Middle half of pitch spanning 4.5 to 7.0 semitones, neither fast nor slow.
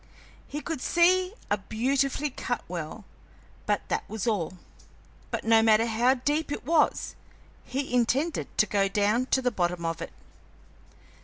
Yes: average, 5.2 semitones; average, 150 wpm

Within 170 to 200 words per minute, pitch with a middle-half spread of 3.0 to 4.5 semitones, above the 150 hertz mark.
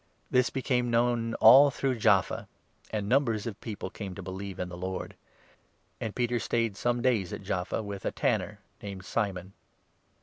No: average, 175 wpm; average, 3.8 semitones; low, 110 Hz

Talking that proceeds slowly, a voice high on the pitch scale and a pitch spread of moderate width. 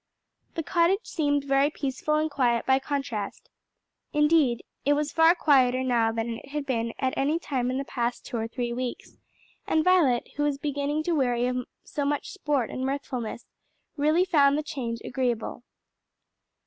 No: average, 170 wpm; very high, 275 Hz; average, 3.4 semitones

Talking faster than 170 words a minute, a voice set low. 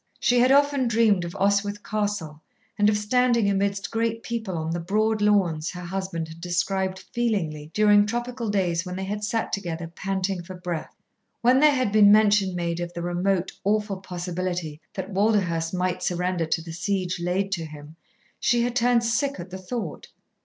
No: average, 180 wpm; high, 195 Hz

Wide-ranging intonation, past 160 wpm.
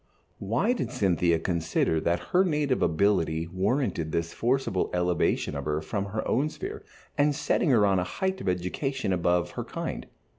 Yes: wide, 8.1 semitones; average, 170 wpm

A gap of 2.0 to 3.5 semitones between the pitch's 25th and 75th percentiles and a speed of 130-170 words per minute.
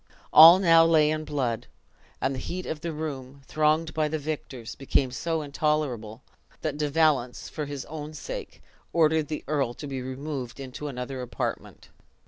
Yes: average, 3.0 semitones; average, 165 wpm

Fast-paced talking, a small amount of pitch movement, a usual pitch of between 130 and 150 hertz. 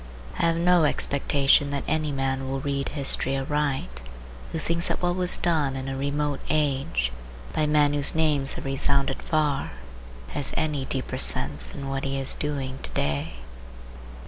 No: average, 165 wpm; narrow, 1.9 semitones; medium, 140 Hz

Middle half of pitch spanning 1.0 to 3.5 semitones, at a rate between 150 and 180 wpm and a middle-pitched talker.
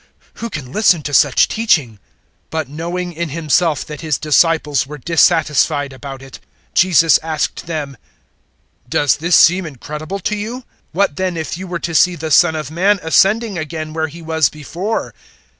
Yes: average, 3.0 semitones; average, 175 wpm; medium, 160 Hz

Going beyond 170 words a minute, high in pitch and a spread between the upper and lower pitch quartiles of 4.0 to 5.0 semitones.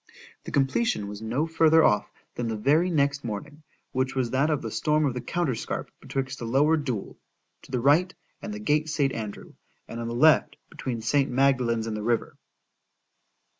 No: average, 180 wpm; low, 135 Hz; average, 4.5 semitones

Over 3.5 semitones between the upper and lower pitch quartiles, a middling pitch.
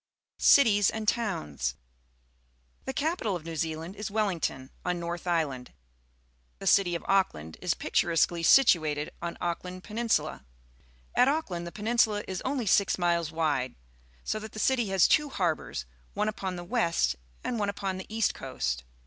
Yes: average, 5.2 semitones; medium, 180 Hz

